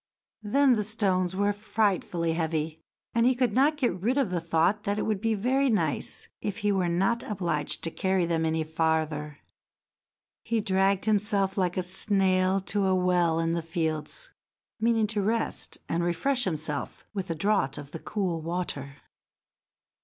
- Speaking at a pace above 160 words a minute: Yes, average, 170 wpm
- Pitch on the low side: No, high, 190 Hz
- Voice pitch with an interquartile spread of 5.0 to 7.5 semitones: No, average, 4.4 semitones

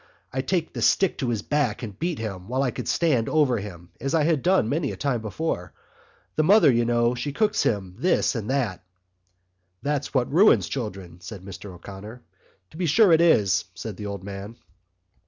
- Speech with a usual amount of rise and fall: No, wide, 7.0 semitones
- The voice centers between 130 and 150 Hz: No, low, 120 Hz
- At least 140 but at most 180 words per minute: No, average, 195 wpm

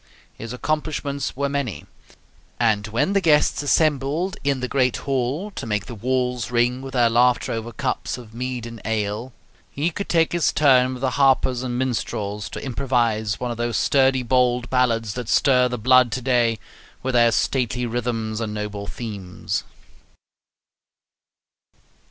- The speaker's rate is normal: Yes, average, 155 wpm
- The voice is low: Yes, low, 125 Hz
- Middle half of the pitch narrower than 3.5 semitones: Yes, average, 2.7 semitones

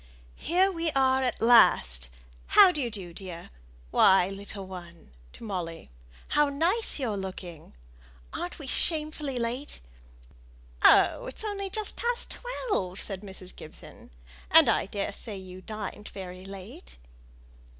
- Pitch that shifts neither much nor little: No, wide, 7.5 semitones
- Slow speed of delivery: Yes, slow, 130 wpm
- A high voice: Yes, high, 205 Hz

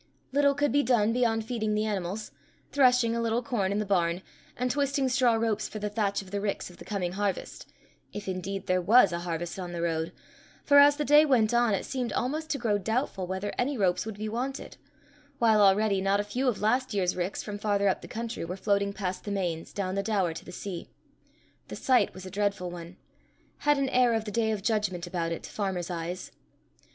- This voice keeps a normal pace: No, fast, 225 wpm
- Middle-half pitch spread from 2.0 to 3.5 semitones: No, average, 4.2 semitones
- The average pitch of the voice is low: No, high, 205 Hz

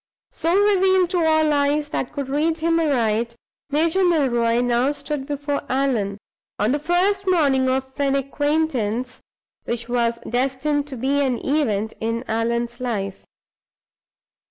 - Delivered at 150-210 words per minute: No, slow, 135 wpm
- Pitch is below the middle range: No, very high, 275 Hz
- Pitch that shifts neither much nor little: Yes, average, 4.5 semitones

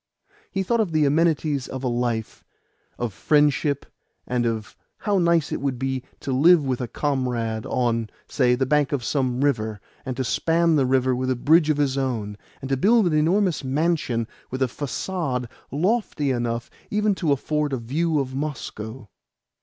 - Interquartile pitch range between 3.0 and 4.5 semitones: Yes, average, 4.0 semitones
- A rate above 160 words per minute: Yes, average, 175 wpm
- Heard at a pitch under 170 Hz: Yes, low, 135 Hz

